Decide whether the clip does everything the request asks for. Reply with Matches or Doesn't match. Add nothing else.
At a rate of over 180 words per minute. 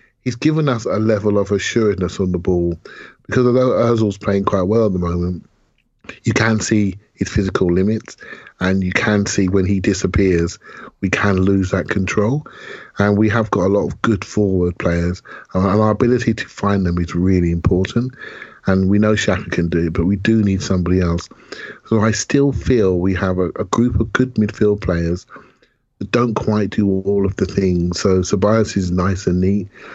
Matches